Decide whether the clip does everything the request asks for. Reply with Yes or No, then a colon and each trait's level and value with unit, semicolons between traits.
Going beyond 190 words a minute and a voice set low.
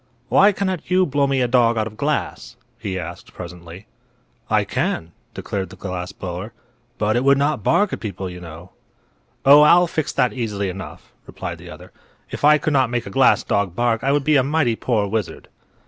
Yes: average, 200 wpm; low, 115 Hz